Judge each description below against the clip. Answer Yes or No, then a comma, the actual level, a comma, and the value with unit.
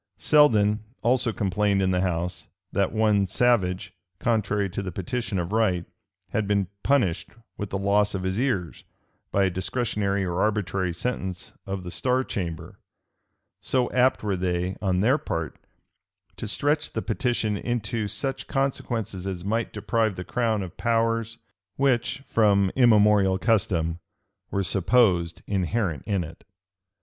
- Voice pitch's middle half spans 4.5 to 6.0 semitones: No, average, 3.8 semitones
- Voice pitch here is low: Yes, low, 100 Hz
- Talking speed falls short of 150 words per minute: Yes, average, 140 wpm